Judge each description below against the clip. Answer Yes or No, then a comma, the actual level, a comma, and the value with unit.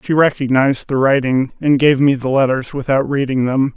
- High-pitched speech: No, low, 135 Hz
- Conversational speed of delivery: Yes, average, 190 wpm